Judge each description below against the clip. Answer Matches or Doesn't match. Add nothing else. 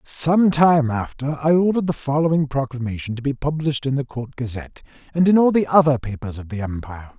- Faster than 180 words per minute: Matches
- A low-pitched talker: Doesn't match